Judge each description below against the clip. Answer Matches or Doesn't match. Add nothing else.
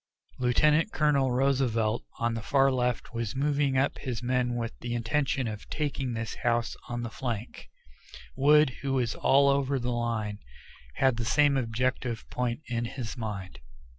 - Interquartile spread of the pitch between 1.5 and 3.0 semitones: Matches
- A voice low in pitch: Matches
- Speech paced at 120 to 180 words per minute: Matches